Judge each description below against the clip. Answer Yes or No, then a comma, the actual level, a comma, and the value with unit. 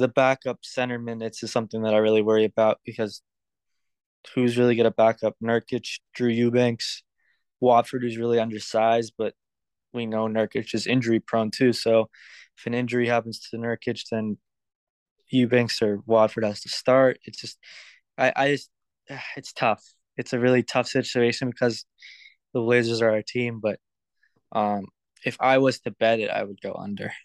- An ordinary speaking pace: Yes, average, 165 wpm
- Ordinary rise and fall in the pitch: No, narrow, 2.0 semitones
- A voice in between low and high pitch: No, low, 115 Hz